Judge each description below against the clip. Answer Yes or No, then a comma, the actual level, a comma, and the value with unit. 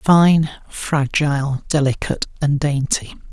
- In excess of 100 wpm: No, slow, 90 wpm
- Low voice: No, medium, 145 Hz